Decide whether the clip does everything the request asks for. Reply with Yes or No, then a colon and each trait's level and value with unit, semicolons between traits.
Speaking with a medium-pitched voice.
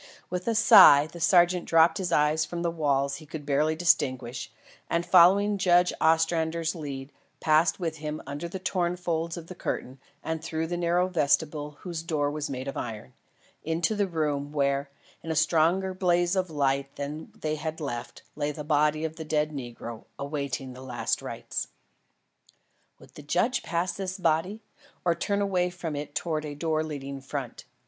Yes: medium, 160 Hz